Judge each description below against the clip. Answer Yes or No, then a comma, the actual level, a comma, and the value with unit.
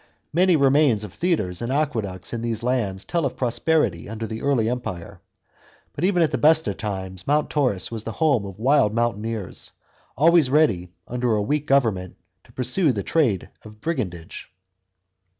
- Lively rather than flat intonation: Yes, wide, 6.3 semitones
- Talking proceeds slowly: No, average, 165 wpm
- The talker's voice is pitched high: No, low, 120 Hz